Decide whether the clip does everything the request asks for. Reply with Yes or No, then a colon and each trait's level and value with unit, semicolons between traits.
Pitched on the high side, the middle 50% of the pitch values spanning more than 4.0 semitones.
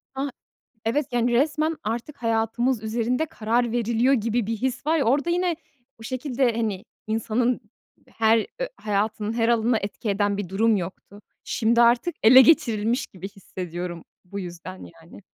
No: high, 230 Hz; average, 3.2 semitones